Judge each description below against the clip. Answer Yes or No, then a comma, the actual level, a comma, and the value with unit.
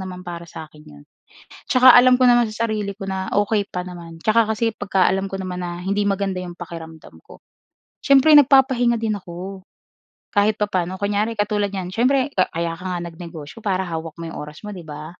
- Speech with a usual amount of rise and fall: Yes, average, 3.8 semitones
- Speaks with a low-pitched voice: No, high, 195 Hz